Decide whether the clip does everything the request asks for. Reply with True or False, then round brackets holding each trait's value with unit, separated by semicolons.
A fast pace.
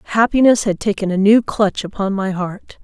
False (190 wpm)